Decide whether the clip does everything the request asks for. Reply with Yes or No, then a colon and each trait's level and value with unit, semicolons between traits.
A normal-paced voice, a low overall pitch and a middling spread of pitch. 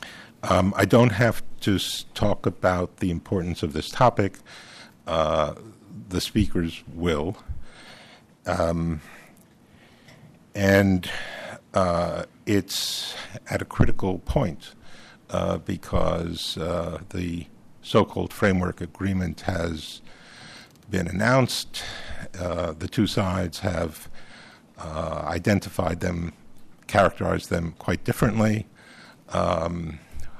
No: slow, 95 wpm; very low, 90 Hz; average, 3.1 semitones